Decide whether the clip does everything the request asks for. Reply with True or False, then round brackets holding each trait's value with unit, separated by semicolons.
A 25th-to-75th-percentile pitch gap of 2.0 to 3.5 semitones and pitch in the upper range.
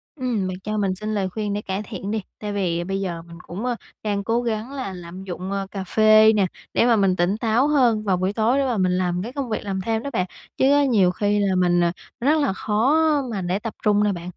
True (3.1 semitones; 205 Hz)